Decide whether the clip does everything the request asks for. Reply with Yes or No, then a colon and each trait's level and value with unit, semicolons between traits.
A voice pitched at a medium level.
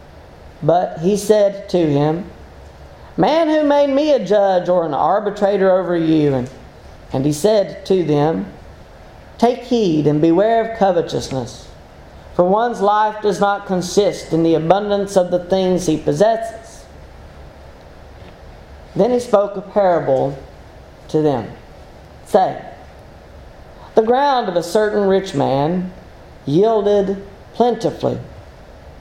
Yes: medium, 175 Hz